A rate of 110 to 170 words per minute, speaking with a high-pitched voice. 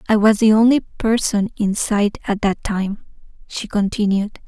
Yes: average, 160 wpm; high, 210 Hz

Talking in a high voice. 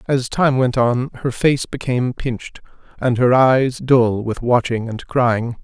No: low, 125 Hz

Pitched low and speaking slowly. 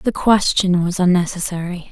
No: medium, 180 Hz; slow, 125 wpm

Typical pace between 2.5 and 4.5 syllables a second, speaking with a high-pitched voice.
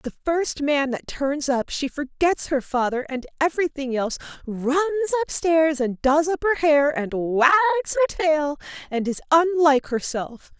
Yes: 4.4 syllables/s; very high, 300 Hz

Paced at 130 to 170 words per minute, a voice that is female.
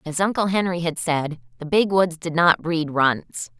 No: average, 200 wpm; female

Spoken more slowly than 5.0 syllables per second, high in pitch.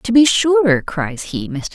Yes: 3.5 syllables/s; high, 205 Hz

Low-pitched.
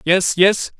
No: medium, 185 Hz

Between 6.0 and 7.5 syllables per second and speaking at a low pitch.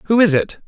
No: 6.4 syllables/s; high, 190 Hz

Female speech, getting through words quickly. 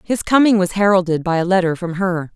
Yes: female; fast, 230 wpm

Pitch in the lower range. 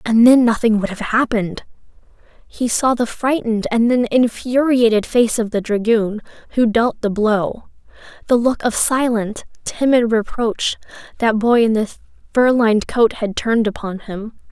No: high, 225 Hz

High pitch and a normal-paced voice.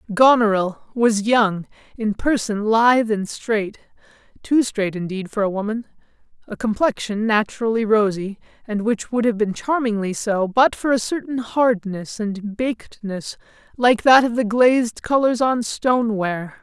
Yes: high, 220 Hz; average, 150 wpm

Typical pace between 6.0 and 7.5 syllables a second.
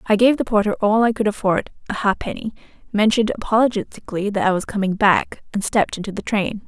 Yes: 6.3 syllables/s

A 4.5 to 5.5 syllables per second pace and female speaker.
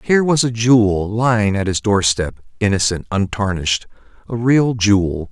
No: 5.0 syllables/s; male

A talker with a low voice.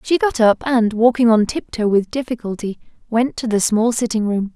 No: high, 225 Hz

